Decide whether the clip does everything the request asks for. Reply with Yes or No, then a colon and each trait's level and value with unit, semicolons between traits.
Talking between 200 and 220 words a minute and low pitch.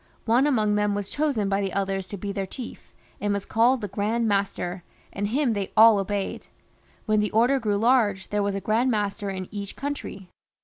No: fast, 205 wpm; high, 205 Hz